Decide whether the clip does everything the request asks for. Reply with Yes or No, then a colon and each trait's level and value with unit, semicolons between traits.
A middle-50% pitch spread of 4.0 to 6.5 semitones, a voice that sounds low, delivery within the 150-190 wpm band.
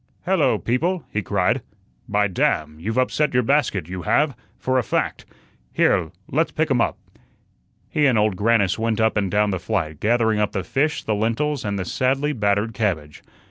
Yes: average, 4.5 semitones; low, 110 Hz; average, 180 wpm